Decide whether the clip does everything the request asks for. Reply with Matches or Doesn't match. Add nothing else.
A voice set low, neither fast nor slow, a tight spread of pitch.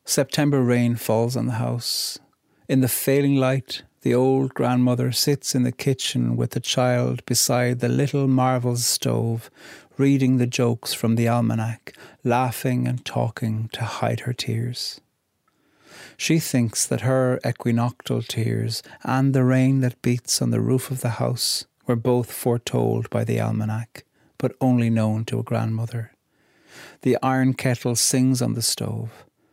Matches